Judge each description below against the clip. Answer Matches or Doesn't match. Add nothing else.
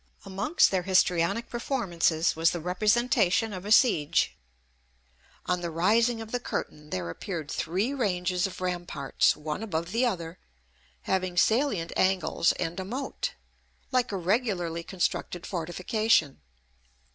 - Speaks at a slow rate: Matches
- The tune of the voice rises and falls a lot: Doesn't match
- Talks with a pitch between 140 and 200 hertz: Matches